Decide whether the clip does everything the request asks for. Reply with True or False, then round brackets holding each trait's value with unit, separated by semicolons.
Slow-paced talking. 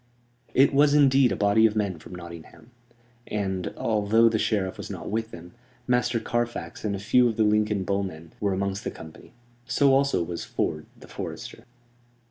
False (175 wpm)